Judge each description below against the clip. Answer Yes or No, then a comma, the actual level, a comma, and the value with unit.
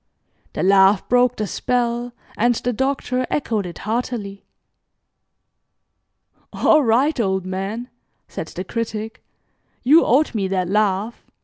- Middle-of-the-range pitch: No, high, 225 Hz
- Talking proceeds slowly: Yes, slow, 120 wpm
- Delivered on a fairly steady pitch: No, average, 4.0 semitones